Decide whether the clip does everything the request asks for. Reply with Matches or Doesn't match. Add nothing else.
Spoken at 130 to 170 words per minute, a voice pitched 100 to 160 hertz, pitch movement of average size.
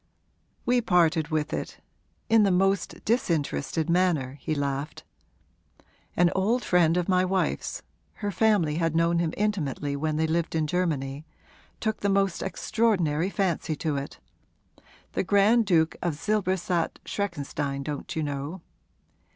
Doesn't match